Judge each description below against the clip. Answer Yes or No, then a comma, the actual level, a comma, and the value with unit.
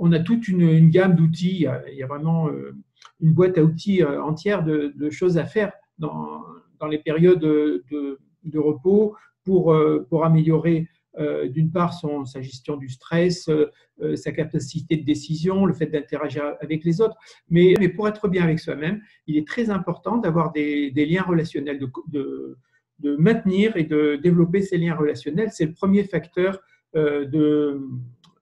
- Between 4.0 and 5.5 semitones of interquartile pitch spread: No, average, 3.3 semitones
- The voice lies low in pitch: No, medium, 160 Hz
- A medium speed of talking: Yes, average, 170 wpm